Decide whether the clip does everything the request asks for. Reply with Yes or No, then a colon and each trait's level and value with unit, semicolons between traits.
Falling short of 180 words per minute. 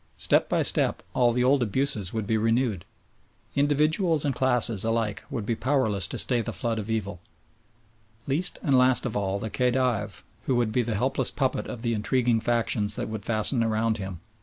No: average, 185 wpm